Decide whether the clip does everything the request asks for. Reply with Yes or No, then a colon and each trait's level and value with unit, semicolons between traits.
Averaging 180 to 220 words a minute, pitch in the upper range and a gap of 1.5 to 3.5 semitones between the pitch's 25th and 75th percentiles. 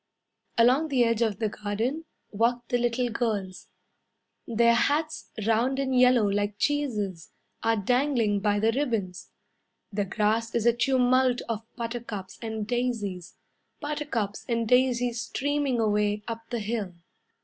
No: slow, 135 wpm; high, 230 Hz; average, 3.1 semitones